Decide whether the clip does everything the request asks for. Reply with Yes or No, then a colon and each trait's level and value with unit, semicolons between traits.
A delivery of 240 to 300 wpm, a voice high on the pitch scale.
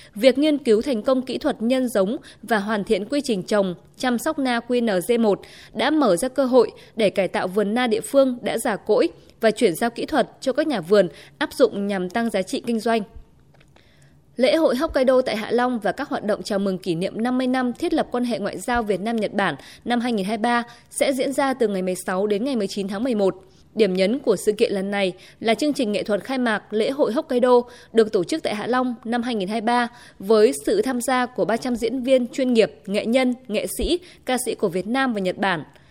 No: average, 225 wpm; high, 235 Hz